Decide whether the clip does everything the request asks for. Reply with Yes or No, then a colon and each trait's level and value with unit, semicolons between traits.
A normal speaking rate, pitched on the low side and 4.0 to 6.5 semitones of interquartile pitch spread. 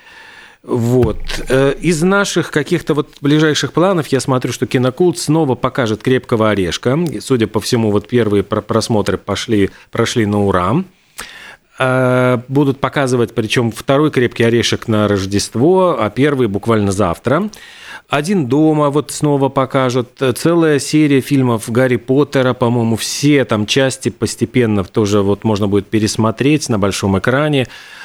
Yes: average, 130 wpm; low, 125 Hz; average, 4.8 semitones